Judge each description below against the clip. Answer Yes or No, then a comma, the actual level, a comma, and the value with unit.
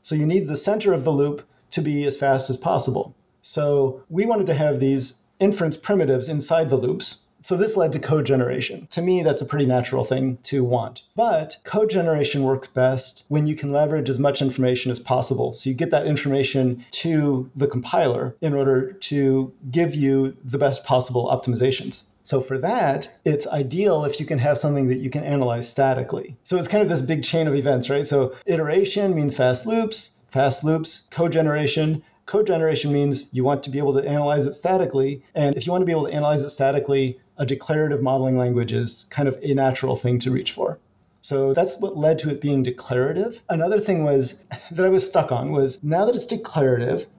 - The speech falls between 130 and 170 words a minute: No, fast, 205 wpm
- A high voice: No, medium, 140 Hz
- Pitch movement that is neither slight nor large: Yes, average, 3.5 semitones